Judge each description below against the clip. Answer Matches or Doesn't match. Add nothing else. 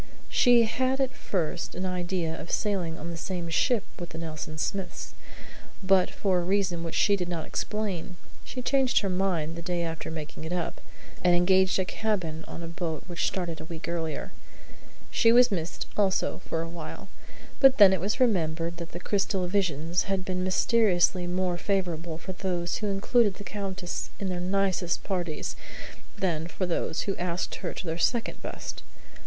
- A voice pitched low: Doesn't match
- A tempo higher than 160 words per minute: Matches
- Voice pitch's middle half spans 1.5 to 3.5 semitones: Matches